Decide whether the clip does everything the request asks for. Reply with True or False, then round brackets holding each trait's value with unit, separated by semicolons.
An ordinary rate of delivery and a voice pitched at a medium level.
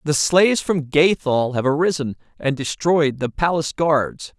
True (150 wpm; 150 Hz)